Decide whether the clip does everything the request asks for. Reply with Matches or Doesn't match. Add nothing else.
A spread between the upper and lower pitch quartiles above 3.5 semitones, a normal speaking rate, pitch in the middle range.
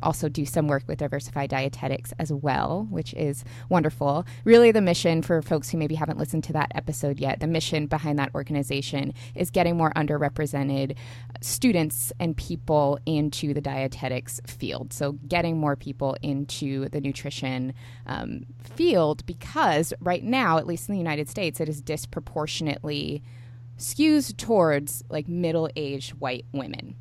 Doesn't match